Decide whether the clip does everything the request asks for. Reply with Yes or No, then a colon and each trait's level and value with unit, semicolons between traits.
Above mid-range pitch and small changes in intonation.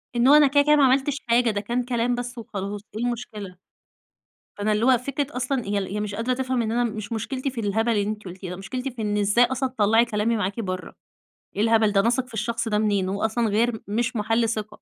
No: high, 230 Hz; average, 3.0 semitones